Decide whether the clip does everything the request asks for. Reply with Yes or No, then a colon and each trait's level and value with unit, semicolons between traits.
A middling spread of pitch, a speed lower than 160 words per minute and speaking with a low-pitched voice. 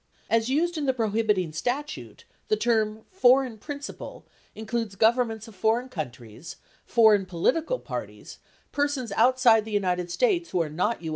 No: average, 4.7 semitones; average, 150 wpm; high, 225 Hz